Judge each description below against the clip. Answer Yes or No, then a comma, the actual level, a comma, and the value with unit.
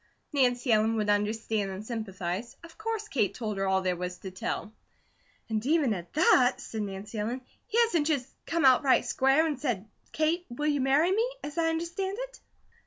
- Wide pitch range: Yes, wide, 7.2 semitones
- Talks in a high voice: Yes, very high, 250 Hz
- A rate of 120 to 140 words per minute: No, average, 190 wpm